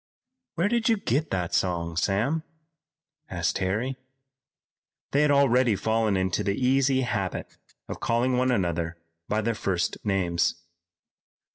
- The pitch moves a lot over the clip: Yes, wide, 5.9 semitones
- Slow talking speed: Yes, slow, 130 wpm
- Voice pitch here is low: Yes, low, 110 Hz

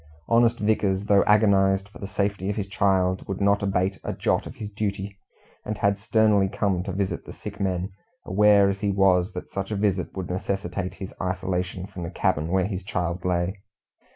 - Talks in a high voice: No, very low, 95 Hz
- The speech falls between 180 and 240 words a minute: Yes, average, 195 wpm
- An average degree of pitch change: No, narrow, 1.6 semitones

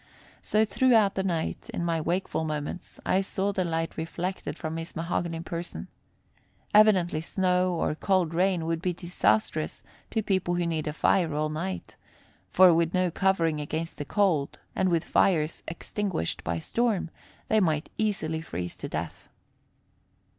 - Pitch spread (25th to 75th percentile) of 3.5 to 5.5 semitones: No, average, 3.0 semitones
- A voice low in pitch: No, medium, 170 Hz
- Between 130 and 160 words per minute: Yes, average, 155 wpm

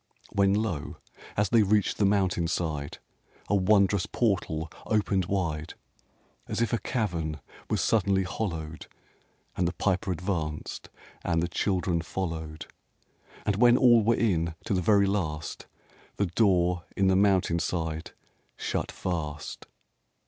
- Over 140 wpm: No, slow, 135 wpm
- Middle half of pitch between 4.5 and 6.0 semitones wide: No, average, 3.8 semitones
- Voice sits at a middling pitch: No, very low, 95 Hz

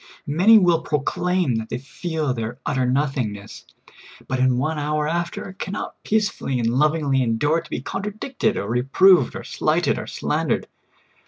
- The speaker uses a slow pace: No, average, 155 wpm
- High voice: No, medium, 150 Hz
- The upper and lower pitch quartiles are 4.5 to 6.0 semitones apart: Yes, wide, 5.4 semitones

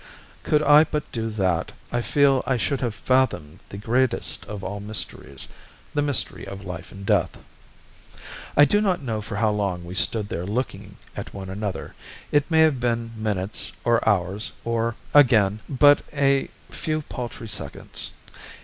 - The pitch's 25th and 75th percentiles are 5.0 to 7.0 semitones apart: Yes, wide, 5.5 semitones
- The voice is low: Yes, low, 115 Hz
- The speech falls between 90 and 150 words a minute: No, average, 160 wpm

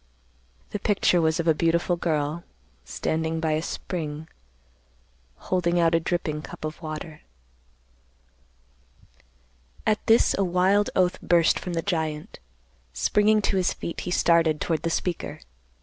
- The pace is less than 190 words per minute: Yes, slow, 135 wpm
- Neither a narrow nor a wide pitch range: No, narrow, 2.3 semitones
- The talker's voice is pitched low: No, medium, 170 Hz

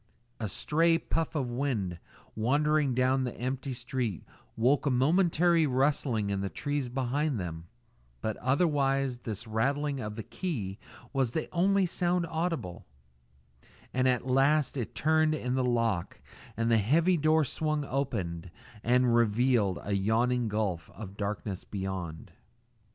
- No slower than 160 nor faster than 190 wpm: No, average, 140 wpm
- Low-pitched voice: Yes, low, 125 Hz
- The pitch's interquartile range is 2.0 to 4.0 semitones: No, wide, 5.4 semitones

